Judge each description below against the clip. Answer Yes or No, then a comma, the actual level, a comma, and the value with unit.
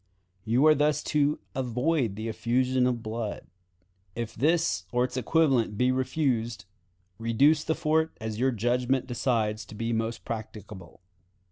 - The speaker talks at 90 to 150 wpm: Yes, average, 140 wpm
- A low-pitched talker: Yes, low, 125 Hz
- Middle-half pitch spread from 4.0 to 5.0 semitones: No, average, 3.5 semitones